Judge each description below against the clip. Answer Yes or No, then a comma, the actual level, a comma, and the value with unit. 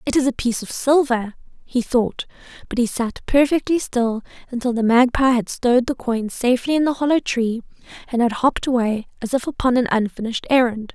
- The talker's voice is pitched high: Yes, high, 245 Hz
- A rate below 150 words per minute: No, average, 190 wpm